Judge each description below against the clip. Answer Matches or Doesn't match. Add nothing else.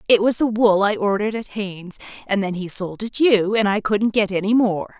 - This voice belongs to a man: Doesn't match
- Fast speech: Matches